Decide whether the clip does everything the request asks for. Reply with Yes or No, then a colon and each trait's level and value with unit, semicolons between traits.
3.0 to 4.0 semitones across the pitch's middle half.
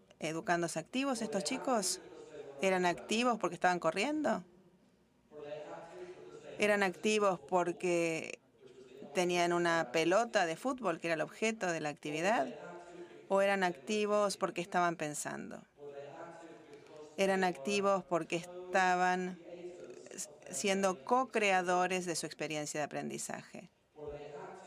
Yes: average, 3.4 semitones